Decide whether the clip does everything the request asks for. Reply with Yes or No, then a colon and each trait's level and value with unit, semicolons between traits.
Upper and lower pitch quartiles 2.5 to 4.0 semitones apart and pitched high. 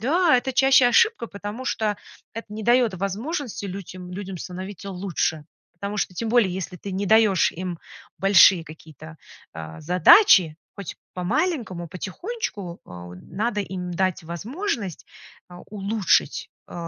No: average, 4.5 semitones; high, 195 Hz